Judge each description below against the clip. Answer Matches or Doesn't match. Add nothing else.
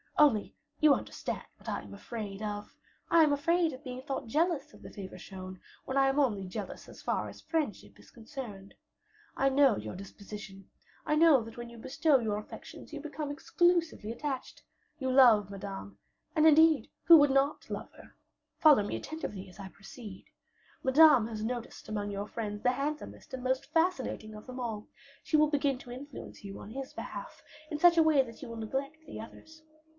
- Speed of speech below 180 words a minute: Doesn't match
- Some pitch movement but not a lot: Doesn't match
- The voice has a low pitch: Doesn't match